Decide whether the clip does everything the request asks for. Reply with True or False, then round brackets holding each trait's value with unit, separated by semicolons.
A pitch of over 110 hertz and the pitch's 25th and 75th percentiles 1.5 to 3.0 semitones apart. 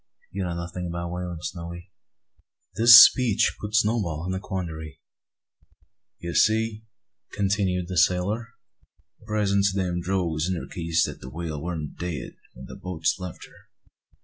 False (90 Hz; 2.7 semitones)